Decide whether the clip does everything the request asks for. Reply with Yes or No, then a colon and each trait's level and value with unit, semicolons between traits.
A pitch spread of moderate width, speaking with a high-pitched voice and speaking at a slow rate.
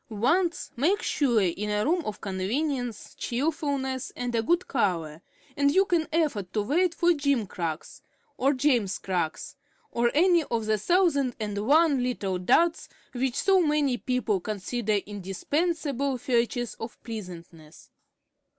No: wide, 6.4 semitones; high, 245 Hz; slow, 130 wpm